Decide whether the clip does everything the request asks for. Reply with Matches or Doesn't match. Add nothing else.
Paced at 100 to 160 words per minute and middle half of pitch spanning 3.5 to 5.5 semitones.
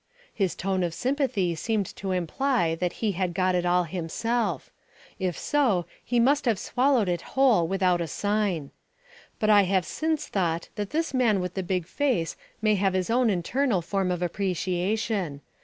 Doesn't match